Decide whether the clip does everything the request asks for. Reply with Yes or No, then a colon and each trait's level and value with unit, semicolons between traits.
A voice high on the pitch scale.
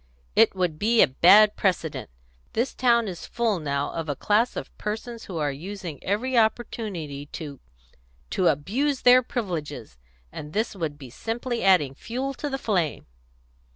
Yes: high, 195 Hz